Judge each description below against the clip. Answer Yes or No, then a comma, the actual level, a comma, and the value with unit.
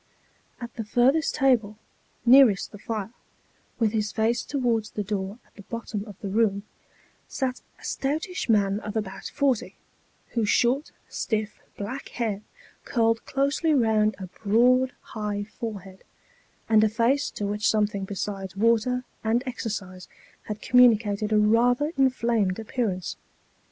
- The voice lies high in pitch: Yes, high, 220 Hz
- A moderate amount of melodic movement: Yes, average, 3.1 semitones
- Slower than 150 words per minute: Yes, average, 140 wpm